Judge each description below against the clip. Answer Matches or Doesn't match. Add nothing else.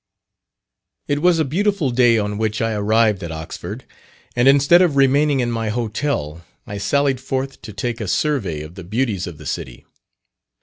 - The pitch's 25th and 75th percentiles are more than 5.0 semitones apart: Matches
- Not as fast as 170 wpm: Doesn't match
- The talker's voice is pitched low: Matches